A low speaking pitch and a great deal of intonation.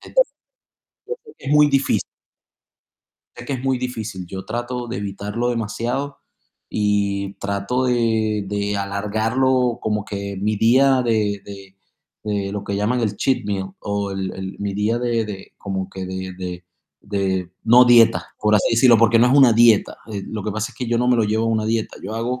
No: low, 110 Hz; average, 3.2 semitones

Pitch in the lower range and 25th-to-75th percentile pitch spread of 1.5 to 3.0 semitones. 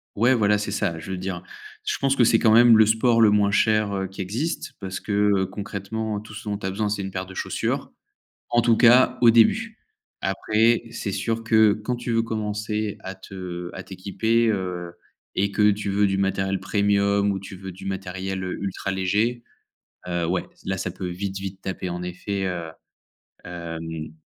Yes: low, 100 Hz; narrow, 2.6 semitones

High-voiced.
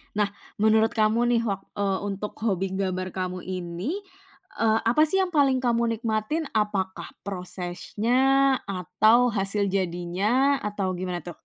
Yes: high, 205 Hz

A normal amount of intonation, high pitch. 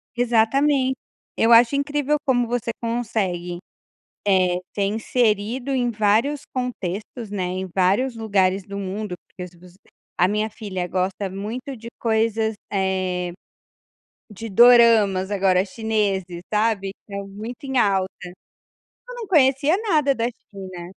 Yes: average, 4.2 semitones; high, 215 Hz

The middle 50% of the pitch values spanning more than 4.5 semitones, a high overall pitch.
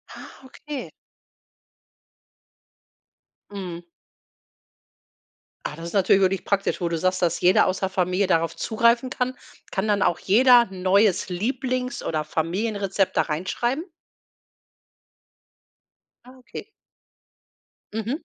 Yes: average, 4.9 semitones; high, 195 Hz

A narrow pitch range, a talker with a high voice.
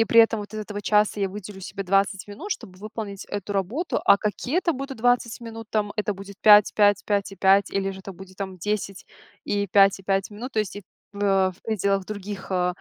Yes: narrow, 1.6 semitones; high, 205 Hz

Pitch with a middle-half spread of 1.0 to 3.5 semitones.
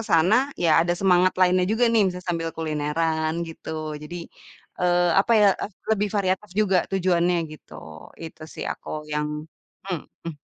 Yes: narrow, 2.6 semitones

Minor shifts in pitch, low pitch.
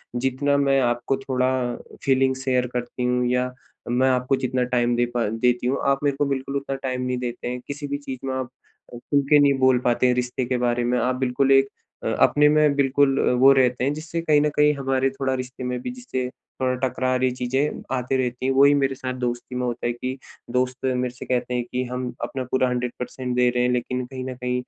Yes: narrow, 1.5 semitones; low, 130 Hz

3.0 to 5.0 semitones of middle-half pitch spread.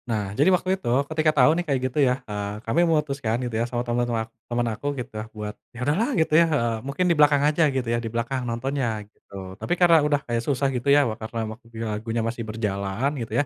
Yes: average, 4.3 semitones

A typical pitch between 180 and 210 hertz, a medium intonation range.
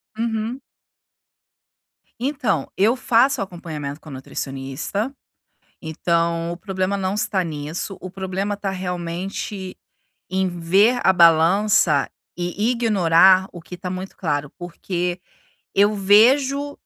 Yes: medium, 185 Hz; average, 3.6 semitones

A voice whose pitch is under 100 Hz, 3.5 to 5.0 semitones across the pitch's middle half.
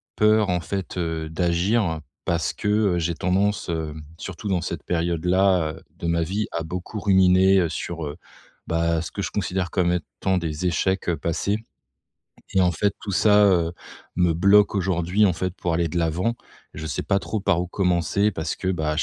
No: very low, 90 Hz; narrow, 2.6 semitones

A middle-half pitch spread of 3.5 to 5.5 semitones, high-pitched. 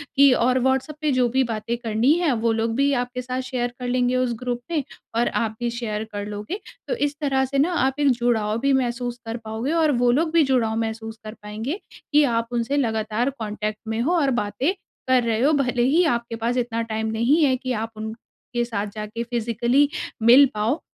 No: average, 3.1 semitones; high, 240 Hz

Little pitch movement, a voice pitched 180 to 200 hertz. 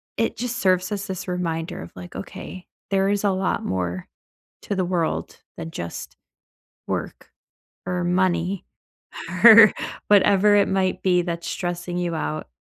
Yes: narrow, 2.1 semitones; medium, 185 Hz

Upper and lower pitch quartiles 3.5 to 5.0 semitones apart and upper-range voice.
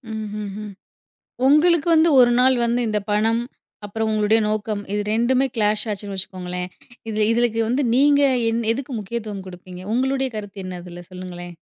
Yes: average, 3.8 semitones; high, 215 Hz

